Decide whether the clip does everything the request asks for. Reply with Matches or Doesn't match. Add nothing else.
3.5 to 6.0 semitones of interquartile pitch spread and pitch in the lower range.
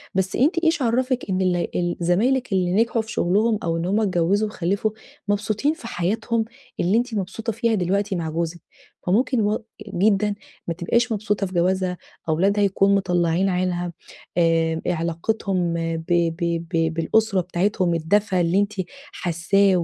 Doesn't match